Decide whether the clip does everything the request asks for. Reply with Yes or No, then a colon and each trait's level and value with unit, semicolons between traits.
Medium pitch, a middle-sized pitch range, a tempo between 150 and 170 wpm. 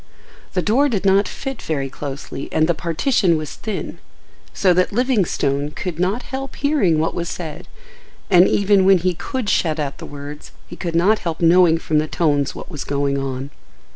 No: medium, 170 Hz; average, 5.0 semitones; average, 185 wpm